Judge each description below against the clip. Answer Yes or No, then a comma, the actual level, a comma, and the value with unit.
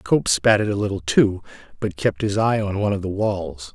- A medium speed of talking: No, fast, 225 wpm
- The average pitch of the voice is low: Yes, low, 100 Hz